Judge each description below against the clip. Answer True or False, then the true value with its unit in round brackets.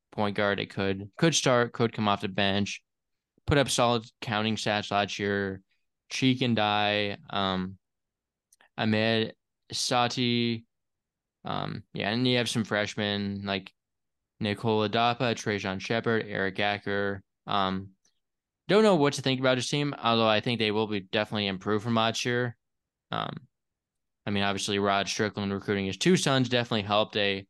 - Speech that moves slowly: False (155 wpm)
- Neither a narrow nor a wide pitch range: True (3.0 semitones)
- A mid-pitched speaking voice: False (105 Hz)